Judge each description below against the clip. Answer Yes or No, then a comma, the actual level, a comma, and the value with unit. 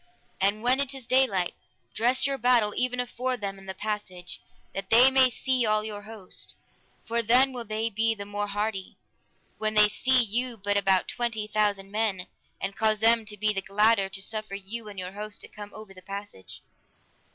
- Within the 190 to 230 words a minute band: Yes, average, 195 wpm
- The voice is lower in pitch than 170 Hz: No, high, 215 Hz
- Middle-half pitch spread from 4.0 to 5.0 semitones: No, average, 2.8 semitones